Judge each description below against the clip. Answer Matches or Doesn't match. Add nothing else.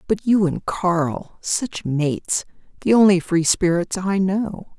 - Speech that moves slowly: Matches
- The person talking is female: Matches